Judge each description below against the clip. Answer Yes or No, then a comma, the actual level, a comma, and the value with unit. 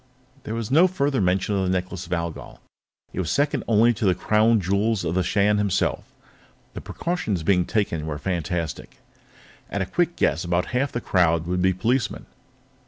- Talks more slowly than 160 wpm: No, average, 180 wpm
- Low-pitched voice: Yes, very low, 95 Hz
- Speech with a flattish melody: No, average, 4.2 semitones